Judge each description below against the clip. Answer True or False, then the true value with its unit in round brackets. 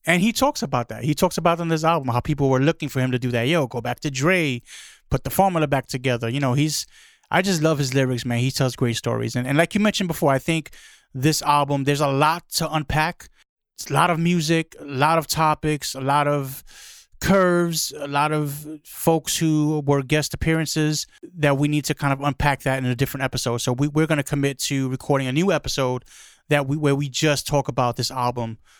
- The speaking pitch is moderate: True (145 Hz)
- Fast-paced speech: True (230 wpm)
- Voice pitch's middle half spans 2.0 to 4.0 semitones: True (3.3 semitones)